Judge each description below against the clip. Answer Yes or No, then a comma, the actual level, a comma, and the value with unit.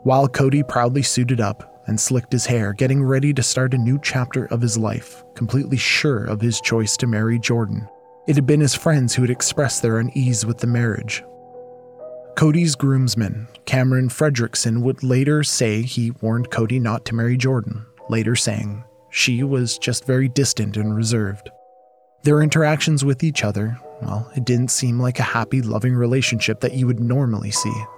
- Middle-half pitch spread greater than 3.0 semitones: No, average, 2.7 semitones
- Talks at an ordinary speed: Yes, average, 175 wpm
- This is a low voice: Yes, low, 125 Hz